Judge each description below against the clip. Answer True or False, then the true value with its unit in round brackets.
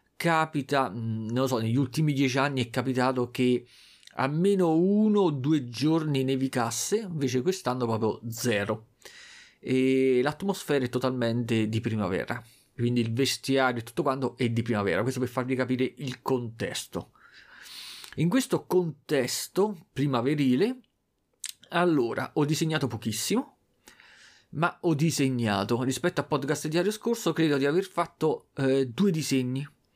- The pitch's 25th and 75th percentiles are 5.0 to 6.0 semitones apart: False (4.5 semitones)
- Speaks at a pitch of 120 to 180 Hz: True (135 Hz)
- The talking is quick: False (130 wpm)